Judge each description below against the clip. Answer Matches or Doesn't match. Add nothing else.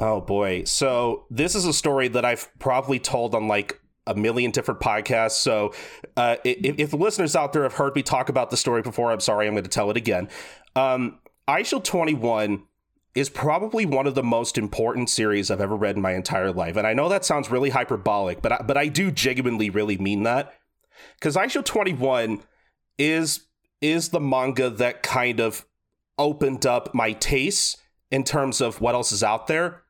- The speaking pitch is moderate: Doesn't match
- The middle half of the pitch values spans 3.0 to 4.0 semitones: Doesn't match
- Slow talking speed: Doesn't match